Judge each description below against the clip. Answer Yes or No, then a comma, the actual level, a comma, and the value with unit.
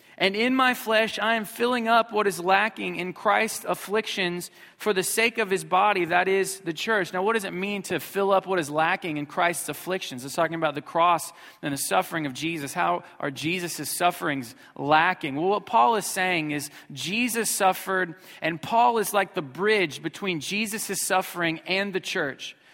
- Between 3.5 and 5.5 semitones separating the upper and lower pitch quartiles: Yes, average, 3.9 semitones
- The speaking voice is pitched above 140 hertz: Yes, medium, 185 Hz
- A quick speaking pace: No, average, 195 wpm